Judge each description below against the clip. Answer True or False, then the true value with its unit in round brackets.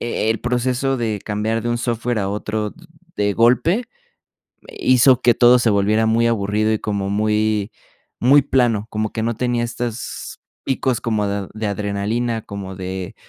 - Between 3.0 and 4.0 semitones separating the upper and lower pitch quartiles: False (2.6 semitones)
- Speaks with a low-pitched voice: True (110 Hz)